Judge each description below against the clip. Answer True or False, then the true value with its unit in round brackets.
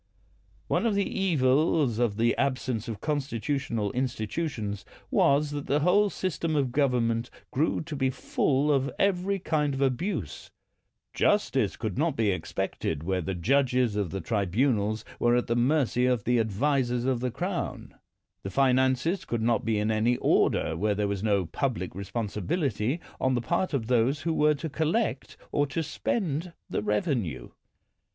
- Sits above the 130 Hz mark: False (125 Hz)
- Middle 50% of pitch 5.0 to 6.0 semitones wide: True (5.3 semitones)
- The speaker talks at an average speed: True (165 wpm)